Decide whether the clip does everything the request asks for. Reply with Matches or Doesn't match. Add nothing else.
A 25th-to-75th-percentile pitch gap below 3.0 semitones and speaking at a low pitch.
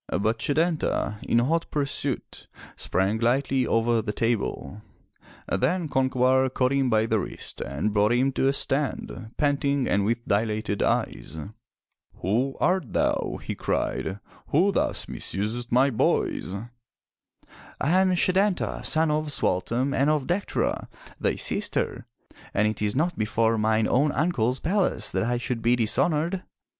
Doesn't match